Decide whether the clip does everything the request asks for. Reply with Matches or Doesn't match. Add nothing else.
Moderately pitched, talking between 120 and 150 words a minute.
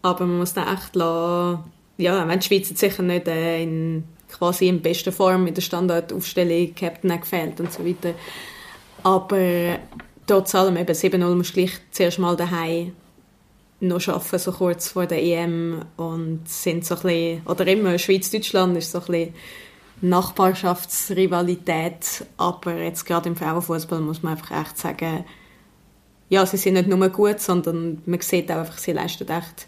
Doesn't match